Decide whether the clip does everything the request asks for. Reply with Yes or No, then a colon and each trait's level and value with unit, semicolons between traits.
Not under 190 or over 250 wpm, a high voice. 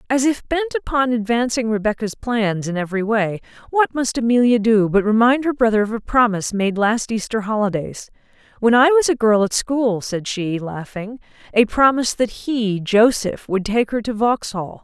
No: average, 170 wpm; high, 225 Hz